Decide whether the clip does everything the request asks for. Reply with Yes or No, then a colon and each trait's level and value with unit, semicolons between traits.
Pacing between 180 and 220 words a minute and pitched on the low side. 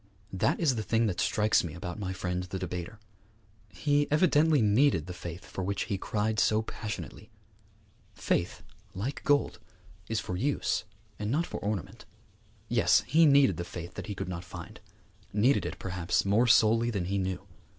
No: average, 170 wpm; low, 105 Hz